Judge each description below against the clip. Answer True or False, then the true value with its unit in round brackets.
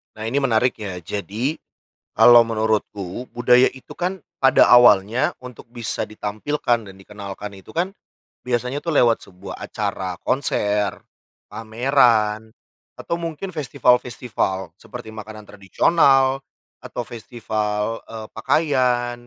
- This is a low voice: True (115 Hz)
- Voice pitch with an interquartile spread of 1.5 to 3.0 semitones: False (3.7 semitones)